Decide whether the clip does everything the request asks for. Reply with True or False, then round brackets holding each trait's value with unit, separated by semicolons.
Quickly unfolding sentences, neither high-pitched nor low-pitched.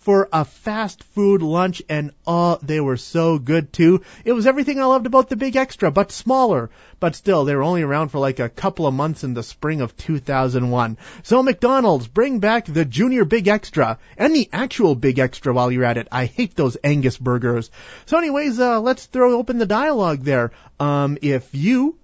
True (210 wpm; 165 Hz)